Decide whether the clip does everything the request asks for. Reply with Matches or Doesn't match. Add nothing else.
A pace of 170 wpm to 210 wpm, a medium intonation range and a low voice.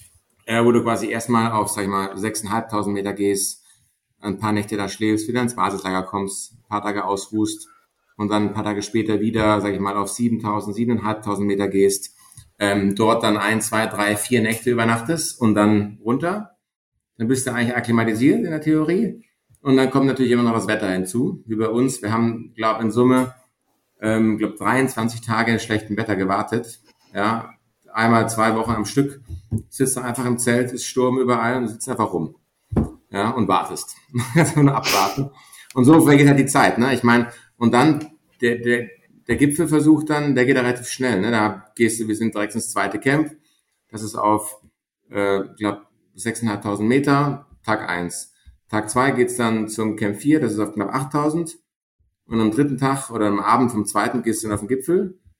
Matches